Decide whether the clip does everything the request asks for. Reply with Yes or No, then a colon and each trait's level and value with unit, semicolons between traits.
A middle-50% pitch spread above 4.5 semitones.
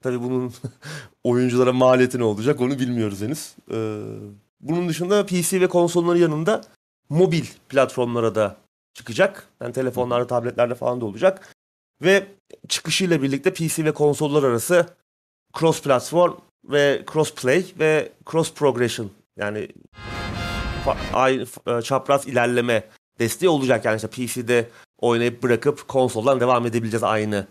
Yes: average, 5.2 semitones